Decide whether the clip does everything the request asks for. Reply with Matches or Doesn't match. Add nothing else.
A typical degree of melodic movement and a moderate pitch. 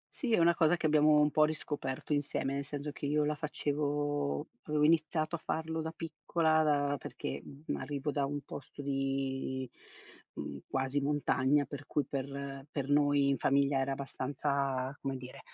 Doesn't match